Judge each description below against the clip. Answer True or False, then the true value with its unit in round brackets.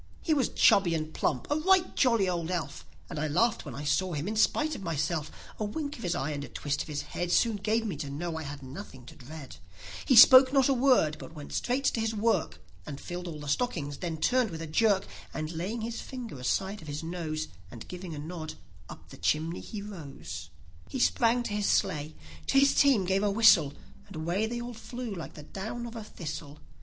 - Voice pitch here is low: False (180 Hz)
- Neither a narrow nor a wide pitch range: False (6.8 semitones)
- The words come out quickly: True (230 wpm)